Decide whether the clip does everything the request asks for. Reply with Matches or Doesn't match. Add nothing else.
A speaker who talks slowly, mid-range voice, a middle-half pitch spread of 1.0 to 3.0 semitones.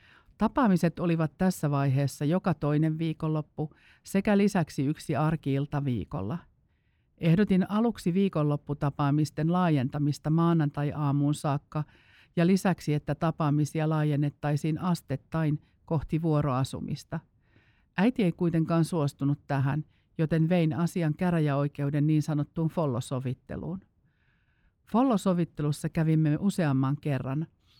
Matches